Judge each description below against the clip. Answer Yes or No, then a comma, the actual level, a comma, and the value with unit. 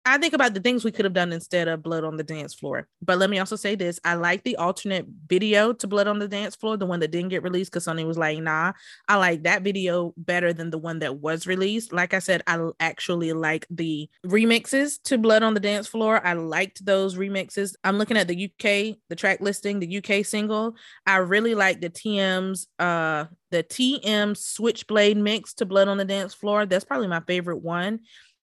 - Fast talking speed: Yes, fast, 220 wpm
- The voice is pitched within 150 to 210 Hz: Yes, high, 190 Hz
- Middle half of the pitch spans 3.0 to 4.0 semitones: Yes, average, 3.3 semitones